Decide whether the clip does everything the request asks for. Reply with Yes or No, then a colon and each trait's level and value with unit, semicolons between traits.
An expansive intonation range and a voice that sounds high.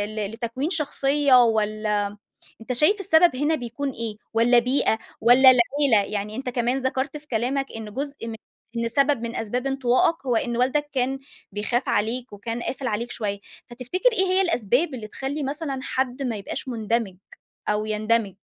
No: average, 3.6 semitones; high, 245 Hz